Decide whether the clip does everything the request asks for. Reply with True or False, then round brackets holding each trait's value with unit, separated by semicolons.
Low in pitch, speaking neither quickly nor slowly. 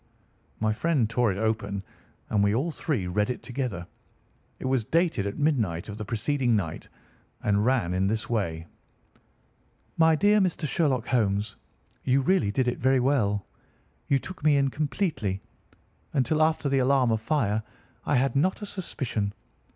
True (125 Hz; 160 wpm)